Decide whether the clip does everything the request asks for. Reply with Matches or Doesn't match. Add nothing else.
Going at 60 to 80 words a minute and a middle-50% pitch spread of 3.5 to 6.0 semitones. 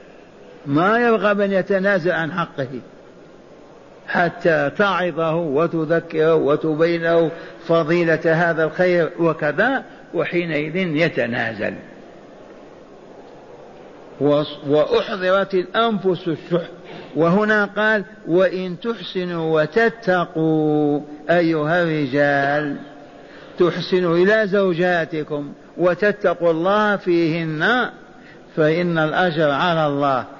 Doesn't match